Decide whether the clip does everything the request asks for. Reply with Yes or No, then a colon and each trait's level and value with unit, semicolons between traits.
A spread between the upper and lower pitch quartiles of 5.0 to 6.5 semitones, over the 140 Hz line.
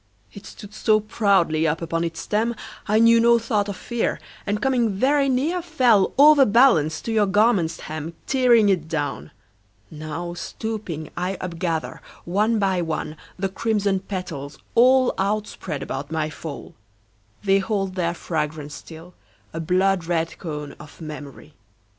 Yes: wide, 5.5 semitones; high, 190 Hz